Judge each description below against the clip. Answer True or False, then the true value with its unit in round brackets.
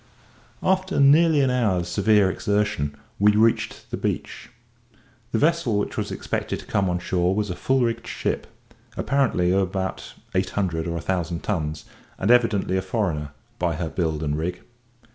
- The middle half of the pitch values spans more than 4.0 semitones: True (4.7 semitones)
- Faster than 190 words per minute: False (165 wpm)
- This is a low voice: True (95 Hz)